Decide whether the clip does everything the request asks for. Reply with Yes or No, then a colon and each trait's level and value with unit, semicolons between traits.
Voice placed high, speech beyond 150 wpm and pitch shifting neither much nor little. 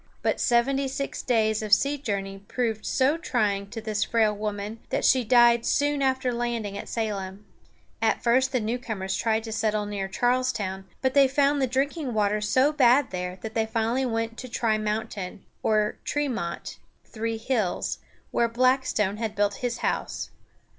Yes: high, 225 Hz; average, 160 wpm; average, 3.4 semitones